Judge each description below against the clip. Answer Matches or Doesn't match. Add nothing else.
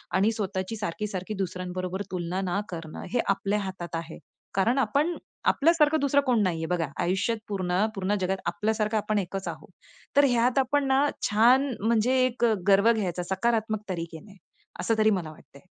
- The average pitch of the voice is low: Doesn't match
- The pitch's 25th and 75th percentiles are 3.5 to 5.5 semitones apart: Matches